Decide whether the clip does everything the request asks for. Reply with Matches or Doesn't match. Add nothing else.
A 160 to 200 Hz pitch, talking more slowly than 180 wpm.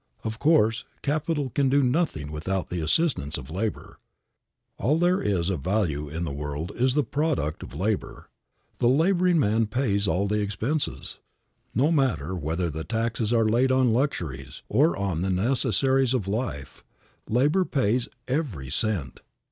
Doesn't match